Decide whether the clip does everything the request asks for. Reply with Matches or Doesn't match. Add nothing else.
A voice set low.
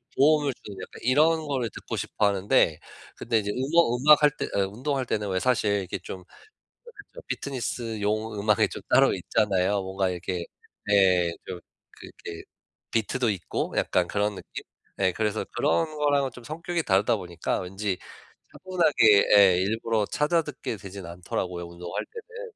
Matches